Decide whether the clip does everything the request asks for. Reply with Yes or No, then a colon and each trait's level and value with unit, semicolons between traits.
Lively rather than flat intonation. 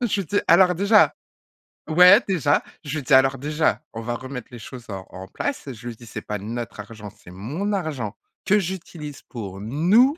Yes: wide, 8.1 semitones